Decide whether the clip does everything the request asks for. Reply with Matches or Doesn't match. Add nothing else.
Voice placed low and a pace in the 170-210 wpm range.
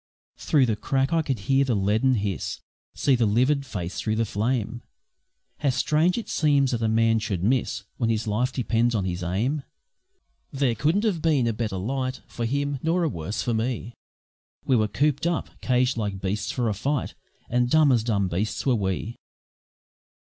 Matches